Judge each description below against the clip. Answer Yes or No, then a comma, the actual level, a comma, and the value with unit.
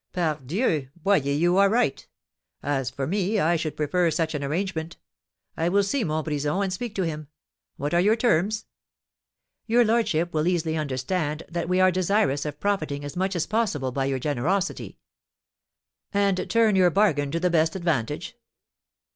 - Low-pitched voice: No, medium, 170 Hz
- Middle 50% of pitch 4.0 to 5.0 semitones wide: Yes, average, 4.7 semitones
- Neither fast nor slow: Yes, average, 165 wpm